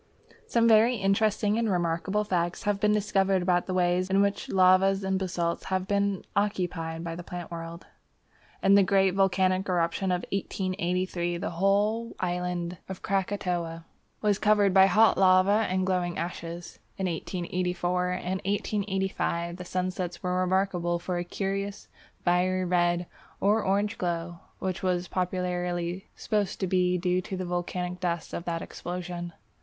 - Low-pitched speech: No, medium, 185 Hz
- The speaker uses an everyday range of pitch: No, narrow, 1.9 semitones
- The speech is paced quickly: No, average, 150 wpm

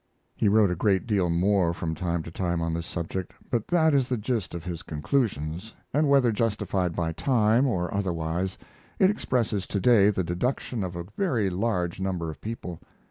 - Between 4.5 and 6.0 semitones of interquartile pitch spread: Yes, average, 5.0 semitones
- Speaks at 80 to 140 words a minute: No, average, 185 wpm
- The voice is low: Yes, very low, 95 Hz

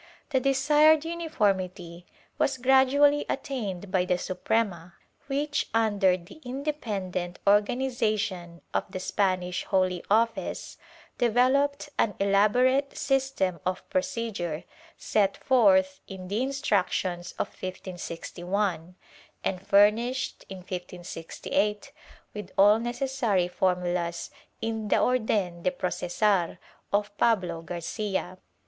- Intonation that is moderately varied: No, wide, 5.8 semitones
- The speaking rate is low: Yes, slow, 105 wpm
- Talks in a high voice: Yes, high, 205 Hz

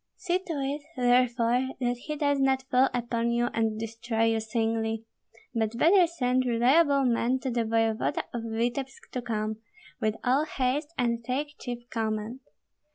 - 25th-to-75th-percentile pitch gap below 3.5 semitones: Yes, average, 2.8 semitones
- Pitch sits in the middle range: No, high, 245 Hz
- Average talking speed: Yes, average, 160 wpm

